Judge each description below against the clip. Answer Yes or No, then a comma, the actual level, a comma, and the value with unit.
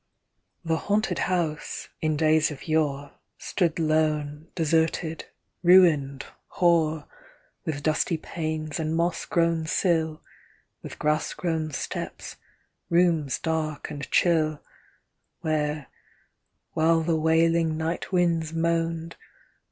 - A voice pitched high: No, medium, 160 Hz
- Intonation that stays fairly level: Yes, narrow, 1.4 semitones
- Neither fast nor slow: No, slow, 105 wpm